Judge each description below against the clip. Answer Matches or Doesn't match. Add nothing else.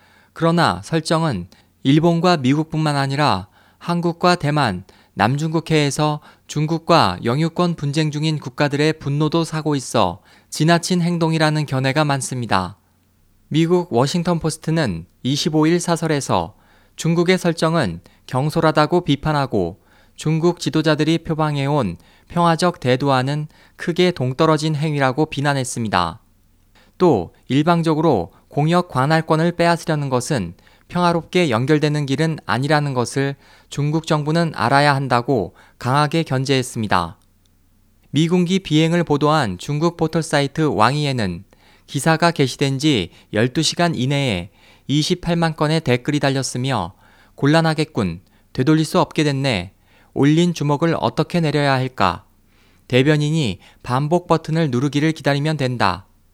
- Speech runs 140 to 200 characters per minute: Doesn't match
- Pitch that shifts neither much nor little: Doesn't match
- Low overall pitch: Doesn't match